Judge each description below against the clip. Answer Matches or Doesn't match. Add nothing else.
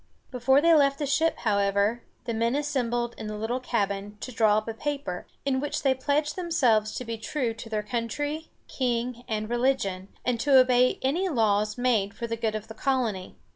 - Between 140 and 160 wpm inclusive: Doesn't match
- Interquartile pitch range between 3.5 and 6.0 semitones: Matches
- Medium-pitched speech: Doesn't match